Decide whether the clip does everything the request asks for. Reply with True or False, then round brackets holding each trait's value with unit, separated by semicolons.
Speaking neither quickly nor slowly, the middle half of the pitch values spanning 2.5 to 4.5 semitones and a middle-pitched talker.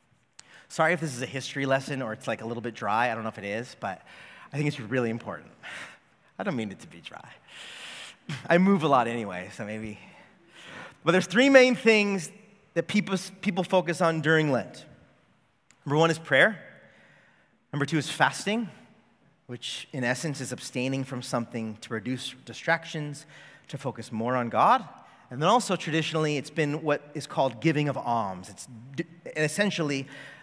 False (175 wpm; 5.3 semitones; 145 Hz)